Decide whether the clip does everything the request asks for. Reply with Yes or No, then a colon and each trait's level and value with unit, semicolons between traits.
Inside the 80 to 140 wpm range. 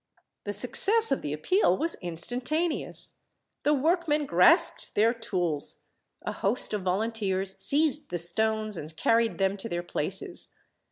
Yes: slow, 135 wpm